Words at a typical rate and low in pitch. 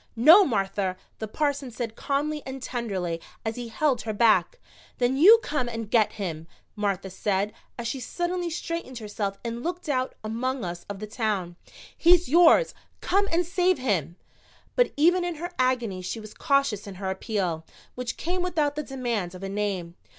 No: average, 175 wpm; high, 240 Hz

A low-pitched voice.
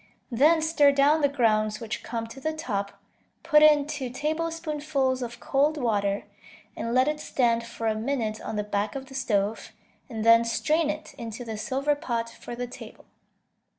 No: very high, 255 Hz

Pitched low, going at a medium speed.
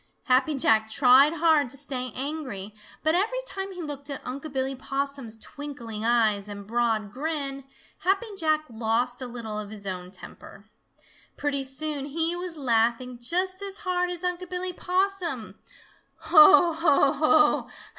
No: very high, 280 Hz; average, 150 wpm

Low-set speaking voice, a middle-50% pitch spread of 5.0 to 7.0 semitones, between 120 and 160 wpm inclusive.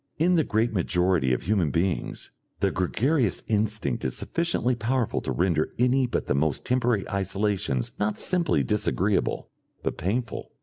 Yes: low, 105 Hz; average, 5.3 semitones; average, 145 wpm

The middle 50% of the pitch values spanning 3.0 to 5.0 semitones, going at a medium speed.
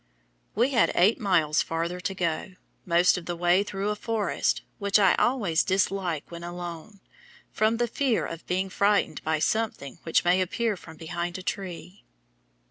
Yes: average, 3.3 semitones; average, 165 wpm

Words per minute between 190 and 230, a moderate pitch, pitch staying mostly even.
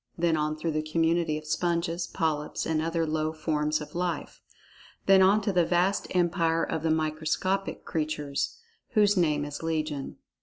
No: average, 160 wpm; medium, 160 Hz; narrow, 2.1 semitones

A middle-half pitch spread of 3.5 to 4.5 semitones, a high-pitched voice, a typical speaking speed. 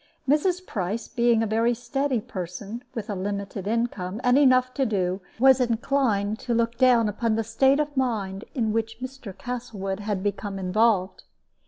Yes: average, 3.9 semitones; high, 225 Hz; average, 160 wpm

